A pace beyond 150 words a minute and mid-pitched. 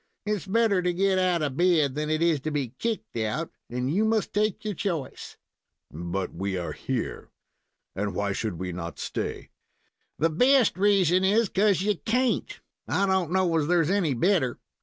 Yes: average, 180 wpm; medium, 175 Hz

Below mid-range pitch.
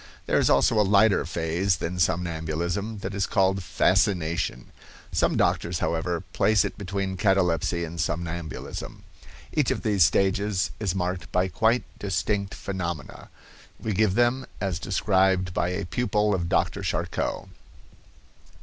Yes: very low, 95 Hz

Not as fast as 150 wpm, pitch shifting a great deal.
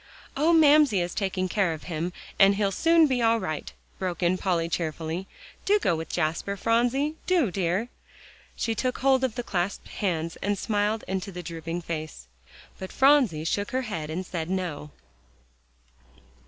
No: average, 170 wpm; wide, 6.0 semitones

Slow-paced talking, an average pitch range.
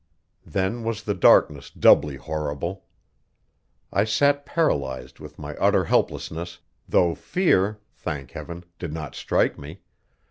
No: slow, 120 wpm; wide, 6.0 semitones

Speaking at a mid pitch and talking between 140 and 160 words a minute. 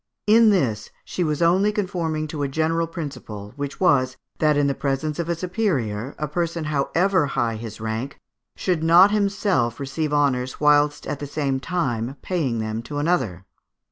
No: medium, 150 Hz; average, 170 wpm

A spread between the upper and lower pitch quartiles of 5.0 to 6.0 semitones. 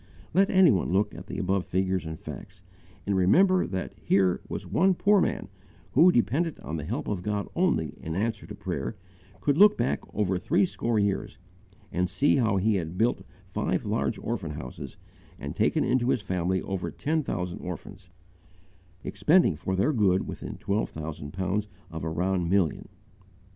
Yes: wide, 5.5 semitones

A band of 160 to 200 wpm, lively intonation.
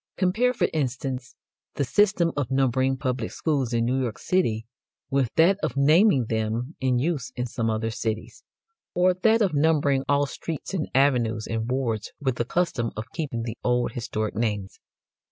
No: average, 170 wpm; average, 4.9 semitones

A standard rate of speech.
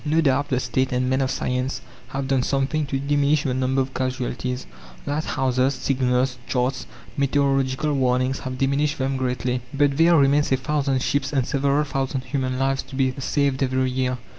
Yes: average, 175 wpm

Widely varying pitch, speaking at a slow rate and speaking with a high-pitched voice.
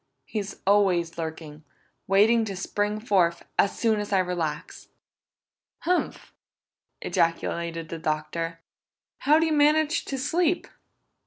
Yes: wide, 5.9 semitones; slow, 115 wpm; high, 195 Hz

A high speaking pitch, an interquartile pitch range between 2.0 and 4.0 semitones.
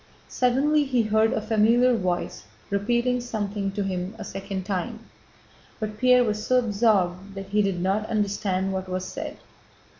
Yes: high, 210 Hz; average, 3.5 semitones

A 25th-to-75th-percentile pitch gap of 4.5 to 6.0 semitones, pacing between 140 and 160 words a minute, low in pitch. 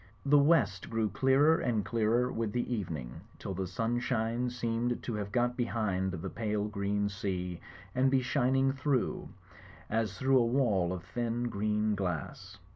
No: average, 3.7 semitones; average, 155 wpm; low, 115 Hz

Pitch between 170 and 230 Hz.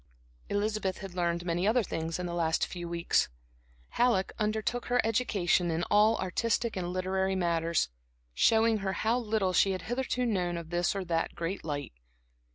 Yes: high, 190 Hz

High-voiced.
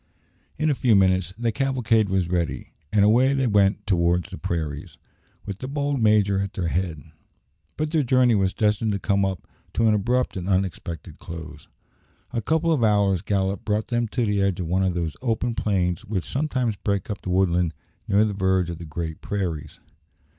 No: low, 100 Hz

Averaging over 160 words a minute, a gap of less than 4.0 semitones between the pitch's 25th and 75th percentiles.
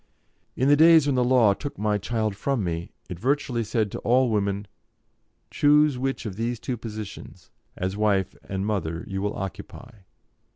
No: average, 170 wpm; average, 4.6 semitones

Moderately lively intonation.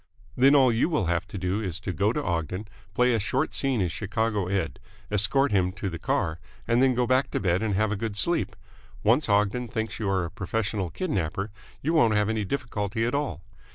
Yes: average, 4.3 semitones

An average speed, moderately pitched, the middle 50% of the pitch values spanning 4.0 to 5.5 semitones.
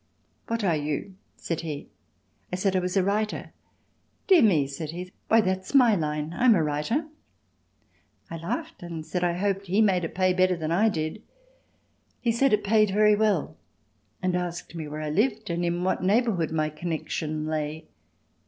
Yes: average, 175 wpm; medium, 180 Hz; average, 4.8 semitones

